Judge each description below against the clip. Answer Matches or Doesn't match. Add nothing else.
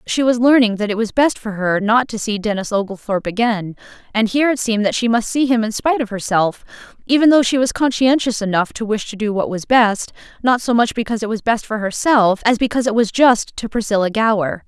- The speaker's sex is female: Matches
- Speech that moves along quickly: Matches